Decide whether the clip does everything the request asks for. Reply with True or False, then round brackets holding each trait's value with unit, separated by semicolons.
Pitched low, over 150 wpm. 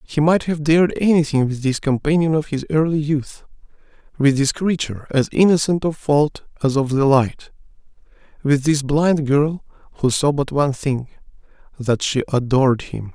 False (145 Hz; 160 wpm)